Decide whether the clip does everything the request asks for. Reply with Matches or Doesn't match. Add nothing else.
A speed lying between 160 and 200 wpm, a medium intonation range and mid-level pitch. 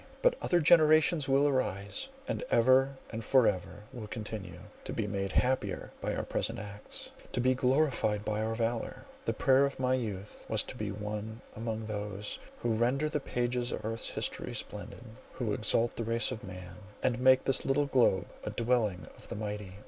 Doesn't match